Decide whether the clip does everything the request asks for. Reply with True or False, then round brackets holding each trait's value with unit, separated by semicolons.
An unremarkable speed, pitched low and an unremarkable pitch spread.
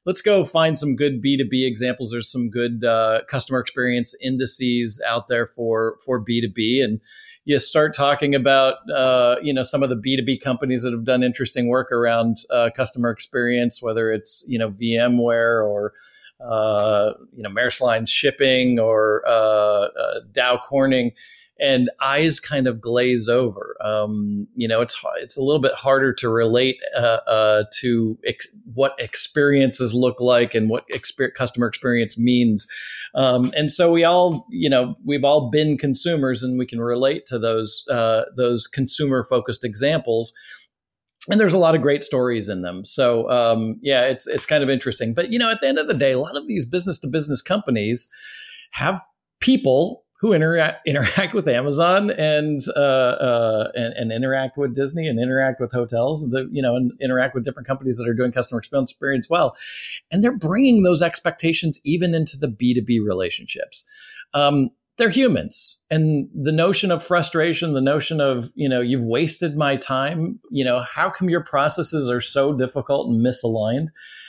True (180 wpm; 130 Hz; 4.0 semitones)